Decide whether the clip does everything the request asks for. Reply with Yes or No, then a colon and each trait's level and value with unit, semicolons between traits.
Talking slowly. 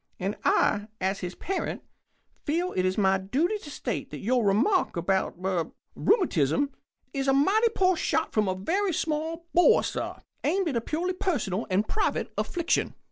No: average, 165 wpm